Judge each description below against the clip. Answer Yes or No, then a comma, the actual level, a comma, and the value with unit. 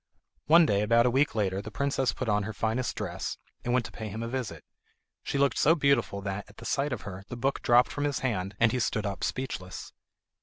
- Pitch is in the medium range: No, low, 115 Hz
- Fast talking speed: Yes, fast, 235 wpm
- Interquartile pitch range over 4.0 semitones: Yes, average, 4.4 semitones